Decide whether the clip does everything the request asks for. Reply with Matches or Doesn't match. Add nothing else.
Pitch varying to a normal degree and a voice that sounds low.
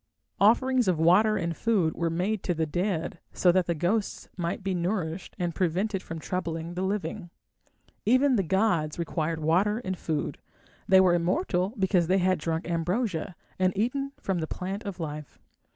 Doesn't match